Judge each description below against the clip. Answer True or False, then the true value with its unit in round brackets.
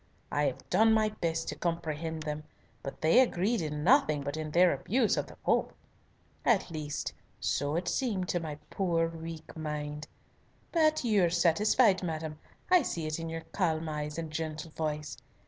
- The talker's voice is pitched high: False (165 Hz)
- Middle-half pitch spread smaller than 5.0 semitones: True (3.4 semitones)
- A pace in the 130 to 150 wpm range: False (175 wpm)